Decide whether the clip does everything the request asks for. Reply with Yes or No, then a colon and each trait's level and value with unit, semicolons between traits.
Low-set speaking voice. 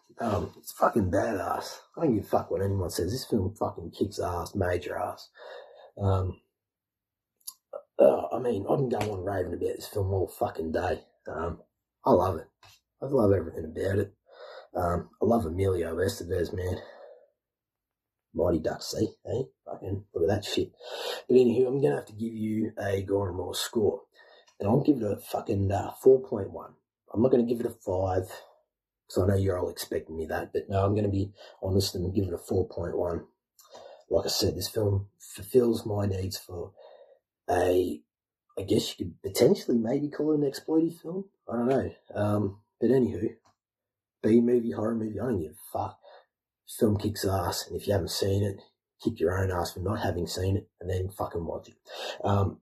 Yes: low, 100 Hz